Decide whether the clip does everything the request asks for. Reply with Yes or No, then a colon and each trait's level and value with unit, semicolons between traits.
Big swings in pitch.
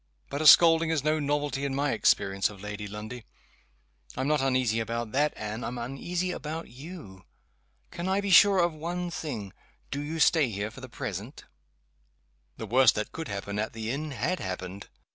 Yes: wide, 6.5 semitones